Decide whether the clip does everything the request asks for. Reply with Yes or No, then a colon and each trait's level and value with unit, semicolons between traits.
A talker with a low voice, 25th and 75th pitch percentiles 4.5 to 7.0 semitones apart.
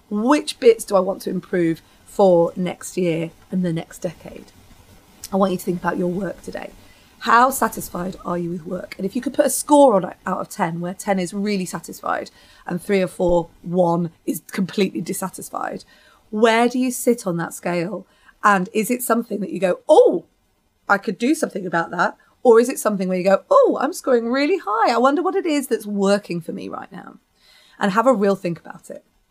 No: high, 200 Hz; average, 5.1 semitones